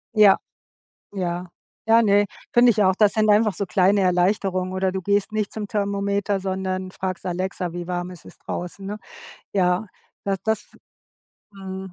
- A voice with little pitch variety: Yes, narrow, 1.9 semitones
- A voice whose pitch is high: Yes, high, 195 Hz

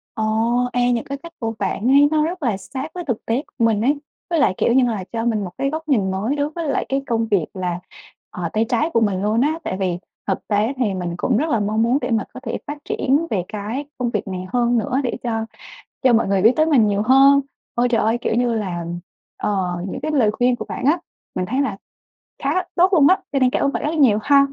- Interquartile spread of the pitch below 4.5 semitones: No, average, 5.0 semitones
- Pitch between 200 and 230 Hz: No, high, 240 Hz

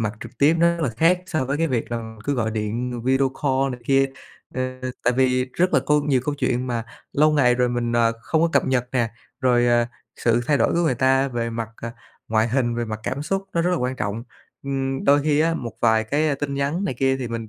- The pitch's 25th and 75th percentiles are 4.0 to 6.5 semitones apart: No, average, 3.4 semitones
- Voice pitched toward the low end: Yes, low, 130 Hz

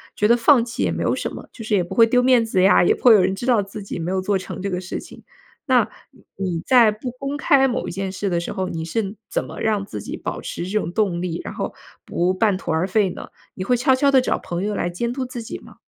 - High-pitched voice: Yes, high, 205 Hz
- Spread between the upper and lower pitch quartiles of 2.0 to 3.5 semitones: No, average, 4.5 semitones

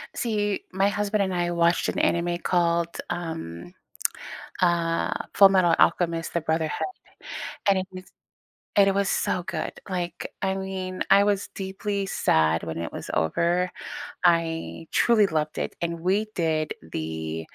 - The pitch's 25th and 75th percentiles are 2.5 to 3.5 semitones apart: Yes, average, 2.8 semitones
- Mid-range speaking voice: Yes, medium, 175 Hz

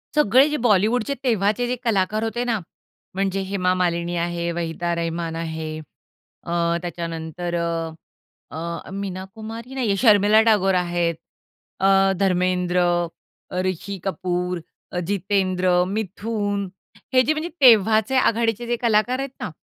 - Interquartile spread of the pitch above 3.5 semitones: Yes, average, 4.1 semitones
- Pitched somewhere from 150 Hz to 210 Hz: Yes, high, 195 Hz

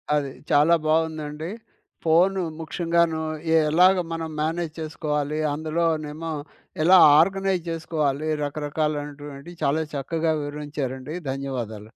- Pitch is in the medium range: Yes, medium, 155 Hz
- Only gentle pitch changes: Yes, narrow, 2.1 semitones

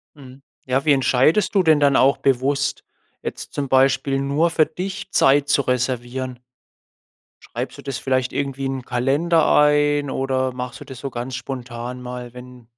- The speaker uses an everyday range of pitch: No, narrow, 2.2 semitones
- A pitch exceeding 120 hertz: Yes, low, 135 Hz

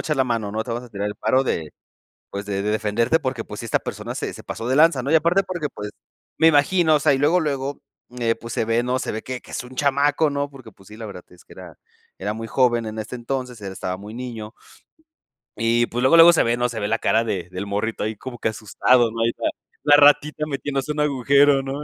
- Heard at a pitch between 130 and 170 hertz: No, low, 120 Hz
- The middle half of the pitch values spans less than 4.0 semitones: No, average, 4.4 semitones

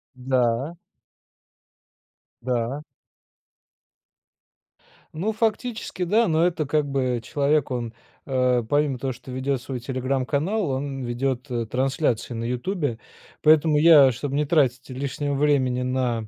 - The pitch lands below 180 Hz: Yes, low, 135 Hz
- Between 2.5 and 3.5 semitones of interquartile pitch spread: Yes, average, 3.0 semitones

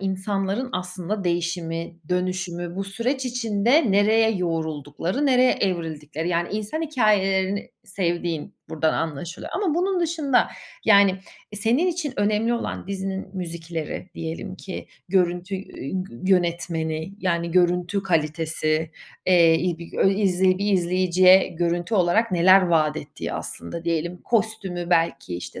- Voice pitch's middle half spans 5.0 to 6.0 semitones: No, average, 3.3 semitones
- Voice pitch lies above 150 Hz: Yes, medium, 185 Hz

